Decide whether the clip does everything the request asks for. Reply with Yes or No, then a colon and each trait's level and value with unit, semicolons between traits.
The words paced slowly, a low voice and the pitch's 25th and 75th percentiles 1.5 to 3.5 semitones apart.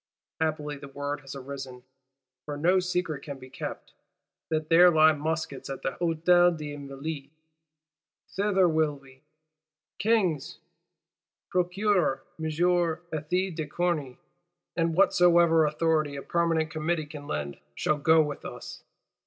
No: slow, 130 wpm; medium, 155 Hz; average, 3.2 semitones